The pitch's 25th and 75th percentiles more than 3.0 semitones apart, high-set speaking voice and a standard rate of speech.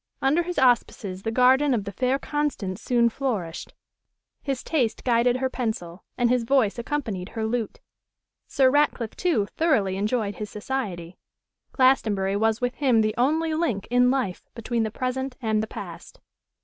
Yes: average, 3.8 semitones; high, 240 Hz; average, 160 wpm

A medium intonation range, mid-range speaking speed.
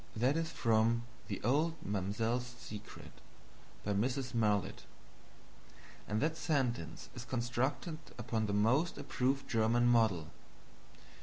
No: average, 3.3 semitones; slow, 110 wpm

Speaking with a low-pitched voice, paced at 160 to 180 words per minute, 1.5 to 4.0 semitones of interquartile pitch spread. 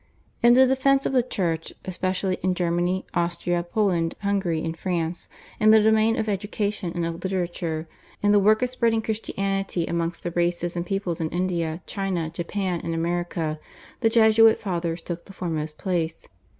No: medium, 180 Hz; average, 165 wpm; average, 3.5 semitones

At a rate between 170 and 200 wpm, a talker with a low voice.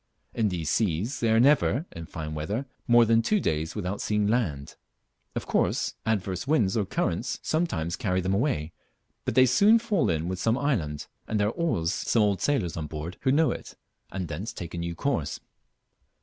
Yes: average, 190 wpm; low, 105 Hz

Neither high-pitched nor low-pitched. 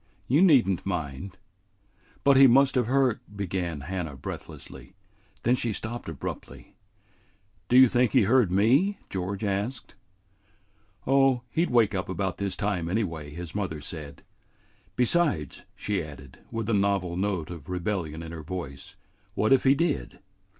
No: low, 100 Hz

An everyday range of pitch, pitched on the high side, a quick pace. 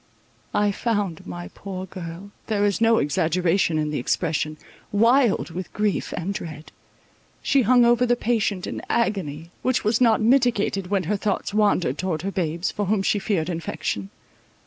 No: average, 4.5 semitones; high, 195 Hz; average, 165 wpm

